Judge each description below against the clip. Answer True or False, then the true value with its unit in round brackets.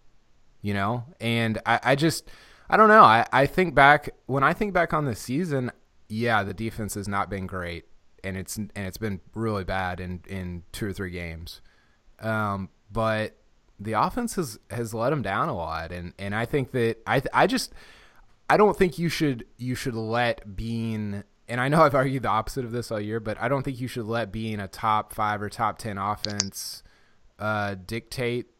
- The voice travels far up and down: False (3.6 semitones)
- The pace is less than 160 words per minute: False (200 wpm)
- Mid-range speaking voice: False (110 Hz)